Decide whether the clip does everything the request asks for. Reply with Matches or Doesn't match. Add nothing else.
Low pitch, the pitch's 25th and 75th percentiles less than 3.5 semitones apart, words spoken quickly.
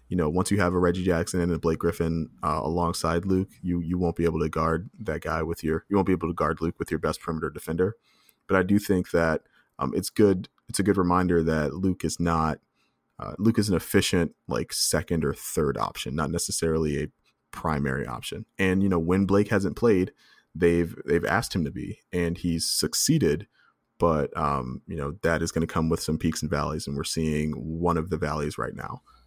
Matches